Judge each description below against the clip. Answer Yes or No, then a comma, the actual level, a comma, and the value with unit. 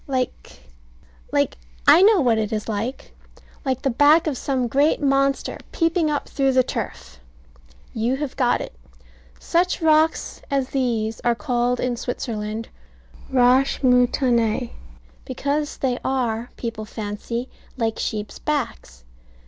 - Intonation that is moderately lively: Yes, average, 3.4 semitones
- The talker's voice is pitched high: Yes, very high, 250 Hz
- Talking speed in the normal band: No, slow, 130 wpm